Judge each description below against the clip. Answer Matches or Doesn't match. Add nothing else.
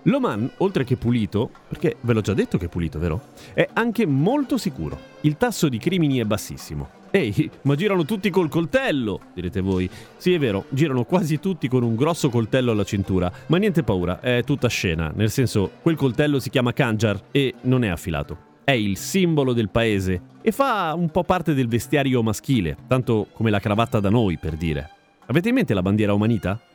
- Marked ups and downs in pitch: Matches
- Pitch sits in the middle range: Doesn't match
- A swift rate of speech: Matches